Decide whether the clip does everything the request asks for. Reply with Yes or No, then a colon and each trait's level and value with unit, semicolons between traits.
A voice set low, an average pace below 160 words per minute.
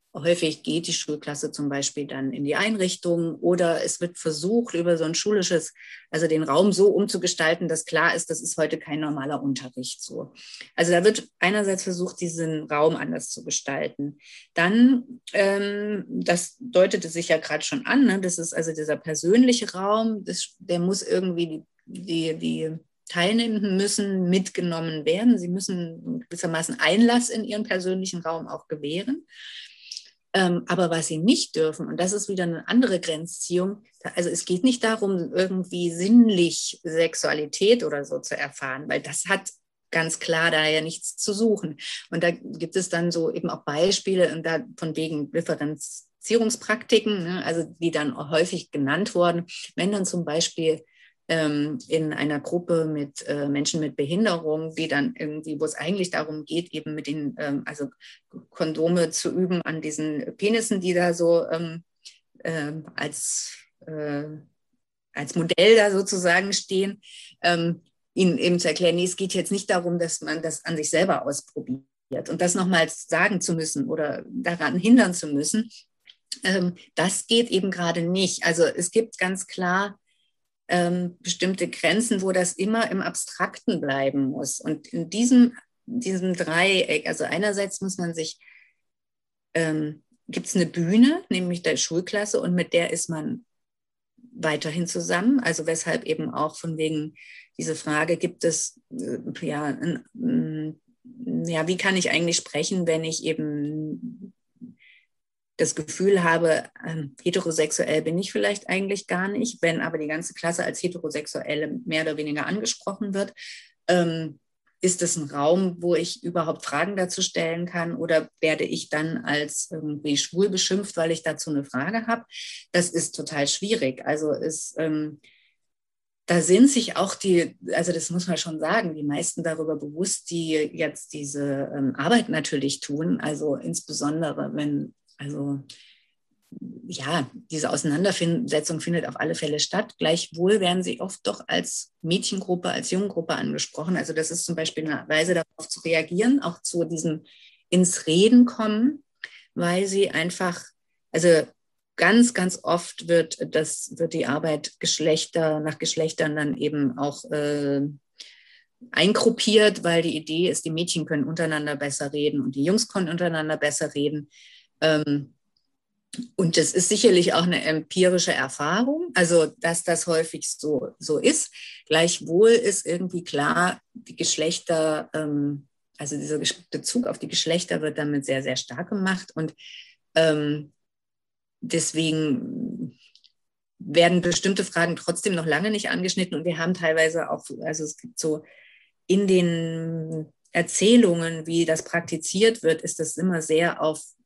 No: medium, 170 Hz; average, 150 wpm